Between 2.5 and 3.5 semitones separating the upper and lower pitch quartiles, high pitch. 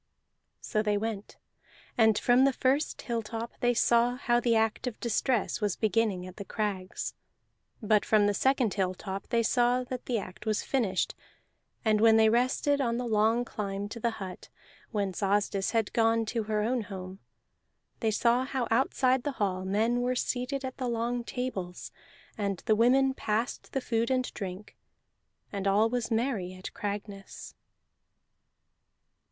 Yes: average, 3.1 semitones; high, 225 Hz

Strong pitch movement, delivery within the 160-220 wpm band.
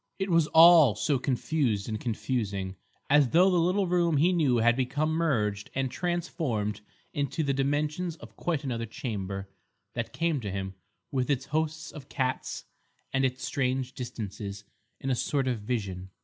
Yes: wide, 6.0 semitones; average, 165 wpm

